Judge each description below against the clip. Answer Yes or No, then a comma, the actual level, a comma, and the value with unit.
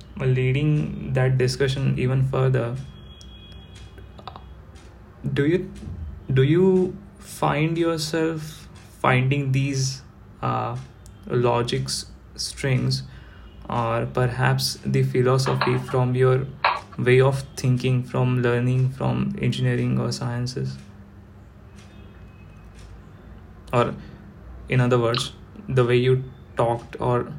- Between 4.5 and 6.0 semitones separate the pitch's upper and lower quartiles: Yes, average, 5.2 semitones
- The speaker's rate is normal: No, slow, 90 wpm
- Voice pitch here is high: No, low, 125 Hz